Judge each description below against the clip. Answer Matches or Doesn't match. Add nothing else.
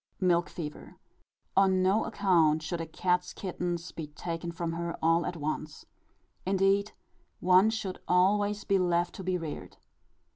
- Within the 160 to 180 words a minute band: Doesn't match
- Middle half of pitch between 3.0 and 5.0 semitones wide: Doesn't match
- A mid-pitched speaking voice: Matches